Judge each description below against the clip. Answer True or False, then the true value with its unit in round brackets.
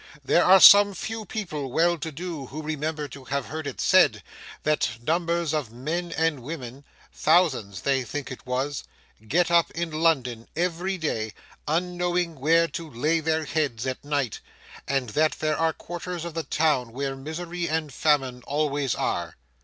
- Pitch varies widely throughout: False (3.9 semitones)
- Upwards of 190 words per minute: False (160 wpm)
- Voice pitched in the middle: True (155 Hz)